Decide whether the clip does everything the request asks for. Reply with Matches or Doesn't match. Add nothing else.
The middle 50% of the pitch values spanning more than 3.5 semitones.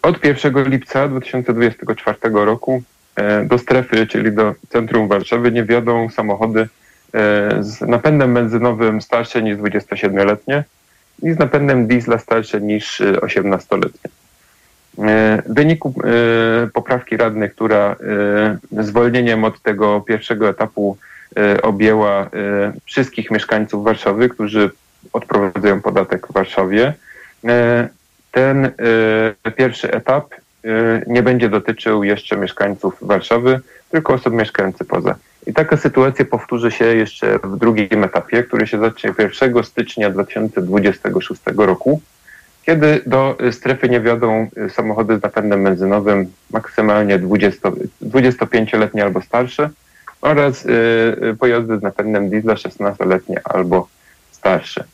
Doesn't match